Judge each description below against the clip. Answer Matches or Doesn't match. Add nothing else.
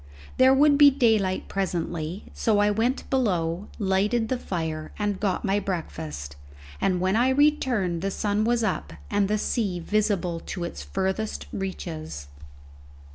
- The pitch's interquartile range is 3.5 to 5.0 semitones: Matches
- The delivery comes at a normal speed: Matches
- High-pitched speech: Matches